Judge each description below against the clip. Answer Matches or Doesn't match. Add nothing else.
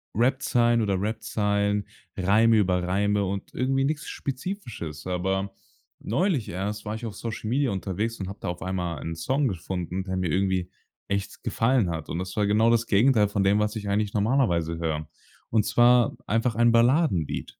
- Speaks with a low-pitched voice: Matches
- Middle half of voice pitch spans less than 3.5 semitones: Doesn't match